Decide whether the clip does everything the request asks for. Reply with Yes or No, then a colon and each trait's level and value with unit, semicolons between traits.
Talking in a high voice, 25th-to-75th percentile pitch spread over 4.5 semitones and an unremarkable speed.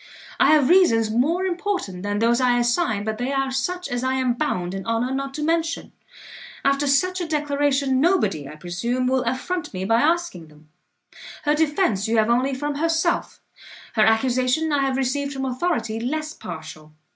Yes: very high, 265 Hz; average, 5.2 semitones; average, 180 wpm